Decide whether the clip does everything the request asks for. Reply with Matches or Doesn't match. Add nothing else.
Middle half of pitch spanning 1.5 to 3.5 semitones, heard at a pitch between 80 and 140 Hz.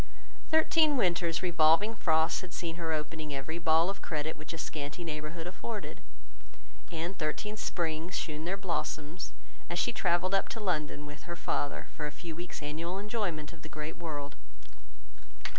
Doesn't match